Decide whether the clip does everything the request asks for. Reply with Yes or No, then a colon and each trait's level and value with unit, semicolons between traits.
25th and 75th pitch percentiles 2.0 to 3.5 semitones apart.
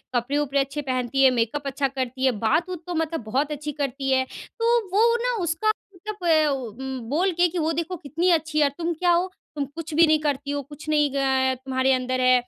No: average, 3.9 semitones